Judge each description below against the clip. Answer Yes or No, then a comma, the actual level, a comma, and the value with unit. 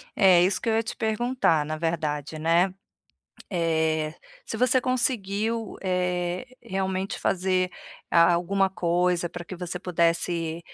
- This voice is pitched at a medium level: Yes, medium, 180 Hz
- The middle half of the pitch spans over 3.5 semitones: No, average, 2.9 semitones